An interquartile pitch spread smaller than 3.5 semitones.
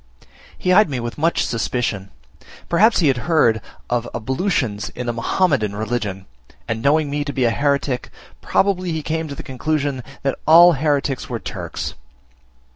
No: average, 5.1 semitones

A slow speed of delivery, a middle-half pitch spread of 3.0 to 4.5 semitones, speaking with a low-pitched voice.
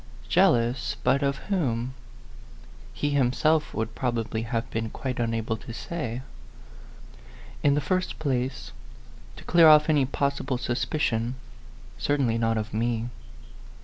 Yes: slow, 120 wpm; average, 3.8 semitones; low, 125 Hz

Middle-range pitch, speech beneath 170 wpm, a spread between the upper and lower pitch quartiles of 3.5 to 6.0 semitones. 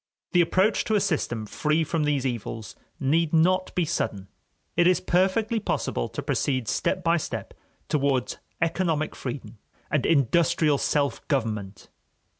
Yes: medium, 155 Hz; average, 140 wpm; average, 4.9 semitones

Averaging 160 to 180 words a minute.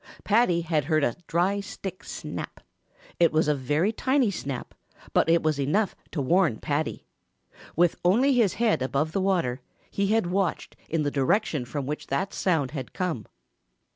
Yes: average, 165 wpm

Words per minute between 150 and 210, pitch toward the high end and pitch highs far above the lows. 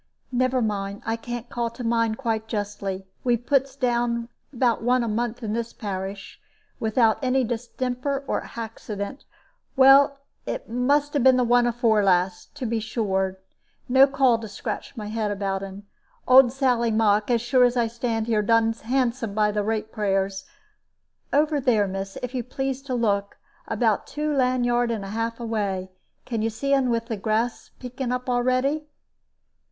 No: average, 170 wpm; high, 235 Hz; average, 2.9 semitones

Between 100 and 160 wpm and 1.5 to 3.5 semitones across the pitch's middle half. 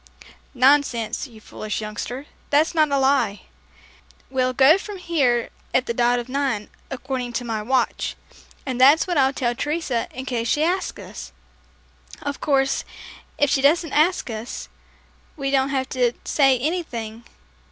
Yes: average, 150 wpm; average, 3.2 semitones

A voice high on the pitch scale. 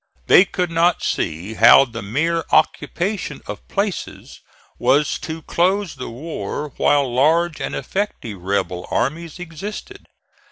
No: medium, 155 Hz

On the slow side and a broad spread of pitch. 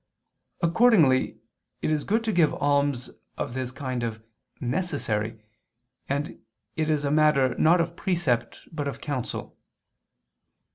No: slow, 130 wpm; average, 4.4 semitones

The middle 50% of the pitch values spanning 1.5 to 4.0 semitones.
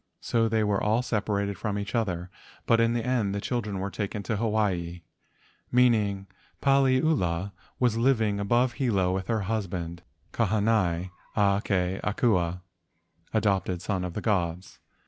Yes: average, 3.5 semitones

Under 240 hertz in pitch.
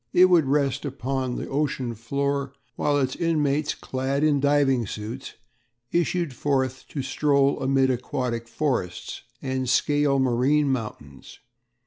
Yes: low, 135 Hz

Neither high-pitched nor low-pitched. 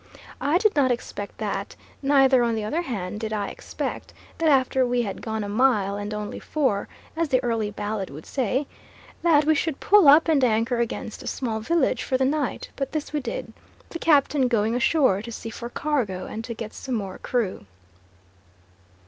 No: high, 245 Hz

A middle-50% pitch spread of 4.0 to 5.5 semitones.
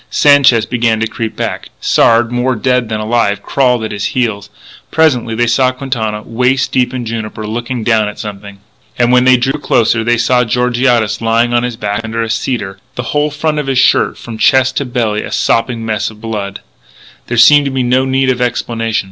No: narrow, 2.4 semitones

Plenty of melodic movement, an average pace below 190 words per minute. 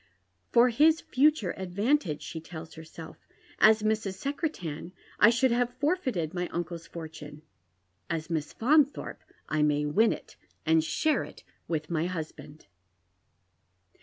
Yes: wide, 7.4 semitones; average, 140 wpm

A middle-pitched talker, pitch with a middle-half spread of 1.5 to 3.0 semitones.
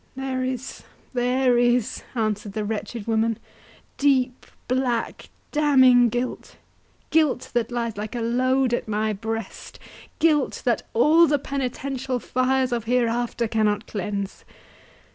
No: high, 245 Hz; narrow, 2.6 semitones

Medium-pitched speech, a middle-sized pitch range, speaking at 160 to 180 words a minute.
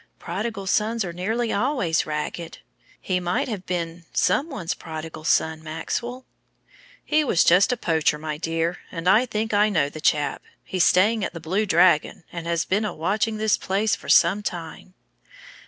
Yes: medium, 180 Hz; average, 4.6 semitones; average, 170 wpm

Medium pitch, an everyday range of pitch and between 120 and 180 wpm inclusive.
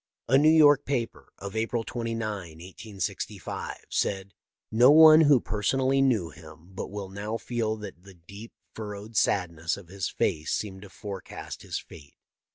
No: low, 105 Hz; average, 3.9 semitones; average, 160 wpm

